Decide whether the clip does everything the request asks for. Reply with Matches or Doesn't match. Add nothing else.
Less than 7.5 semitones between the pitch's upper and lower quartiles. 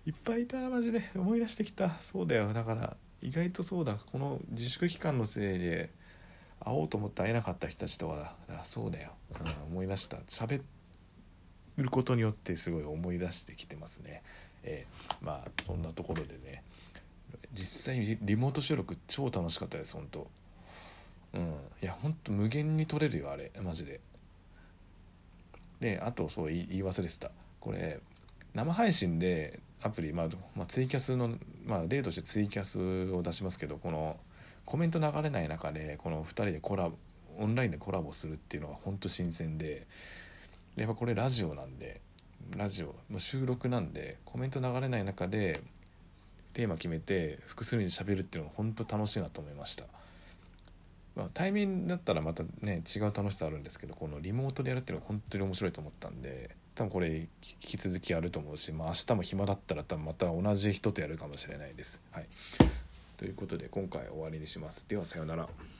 Matches